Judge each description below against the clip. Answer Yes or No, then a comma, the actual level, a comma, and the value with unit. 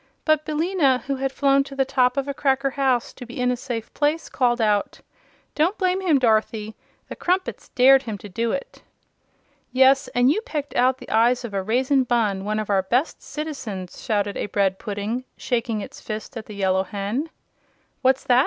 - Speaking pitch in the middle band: No, very high, 250 Hz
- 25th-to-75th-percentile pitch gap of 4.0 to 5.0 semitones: Yes, average, 4.3 semitones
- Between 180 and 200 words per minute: Yes, average, 195 wpm